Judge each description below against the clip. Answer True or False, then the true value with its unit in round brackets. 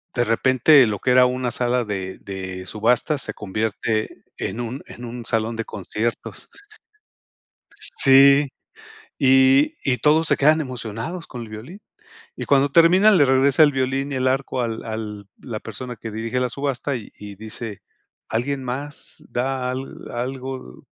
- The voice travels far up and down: False (3.4 semitones)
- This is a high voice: False (125 Hz)